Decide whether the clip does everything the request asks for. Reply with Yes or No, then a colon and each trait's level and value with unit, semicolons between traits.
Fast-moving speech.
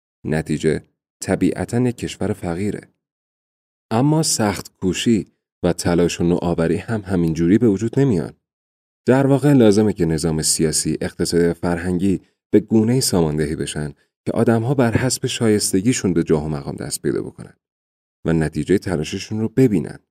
No: average, 145 wpm